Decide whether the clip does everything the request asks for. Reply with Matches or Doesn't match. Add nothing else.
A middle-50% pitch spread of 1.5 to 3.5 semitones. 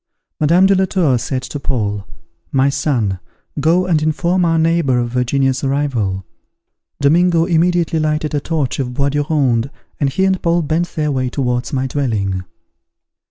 Doesn't match